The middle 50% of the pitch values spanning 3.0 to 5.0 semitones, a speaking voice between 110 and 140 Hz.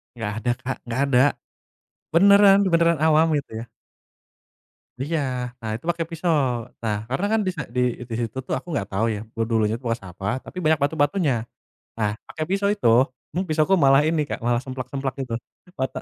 No: wide, 5.6 semitones; low, 135 Hz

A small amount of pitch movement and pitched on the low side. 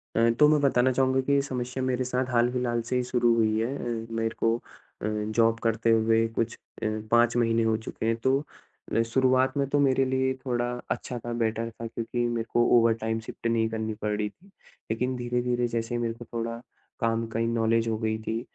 Yes: narrow, 1.8 semitones; low, 115 Hz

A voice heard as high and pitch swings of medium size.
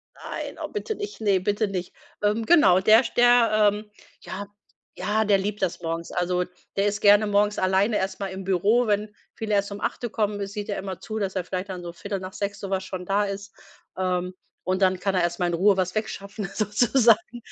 No: high, 200 Hz; narrow, 2.1 semitones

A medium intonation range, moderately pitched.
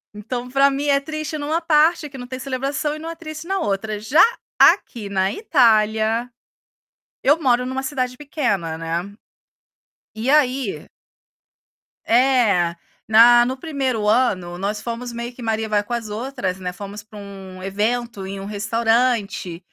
No: average, 4.8 semitones; high, 235 Hz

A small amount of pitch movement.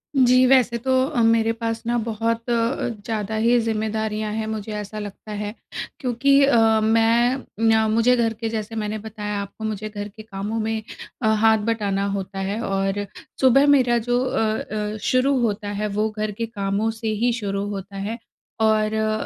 Yes: narrow, 1.7 semitones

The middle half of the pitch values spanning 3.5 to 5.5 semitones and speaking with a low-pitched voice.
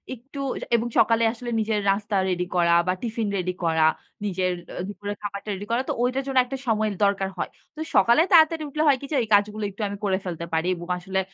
No: average, 4.1 semitones; high, 205 Hz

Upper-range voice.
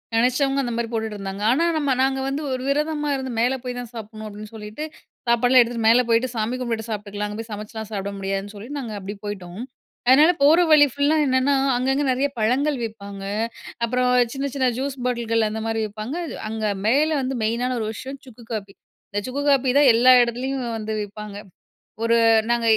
Yes: high, 235 Hz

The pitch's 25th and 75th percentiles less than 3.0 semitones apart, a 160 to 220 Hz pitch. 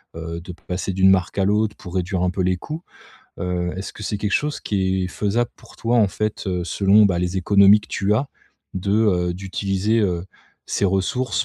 No: narrow, 2.6 semitones; very low, 95 Hz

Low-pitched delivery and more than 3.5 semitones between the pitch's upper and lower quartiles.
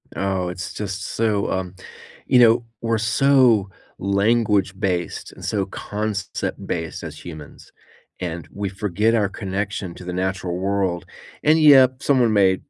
No: low, 100 Hz; average, 3.2 semitones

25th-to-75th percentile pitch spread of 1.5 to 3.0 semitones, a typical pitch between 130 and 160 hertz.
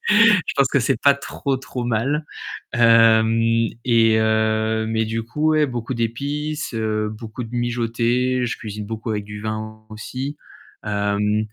No: average, 2.7 semitones; low, 115 Hz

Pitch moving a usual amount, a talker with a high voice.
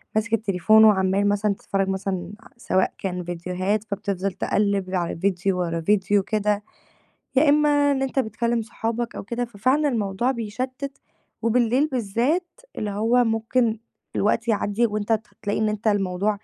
Yes: average, 3.2 semitones; high, 215 Hz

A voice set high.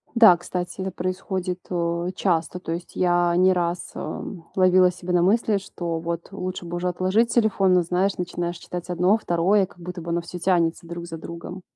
No: medium, 180 Hz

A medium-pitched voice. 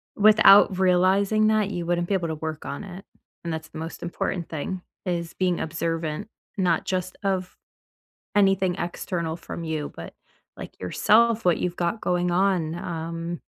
Yes: medium, 175 Hz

